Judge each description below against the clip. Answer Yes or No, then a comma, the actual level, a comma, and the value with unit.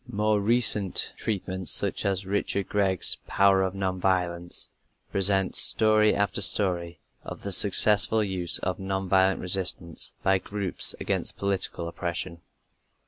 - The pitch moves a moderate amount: No, narrow, 1.7 semitones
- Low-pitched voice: Yes, very low, 95 Hz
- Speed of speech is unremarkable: No, slow, 130 wpm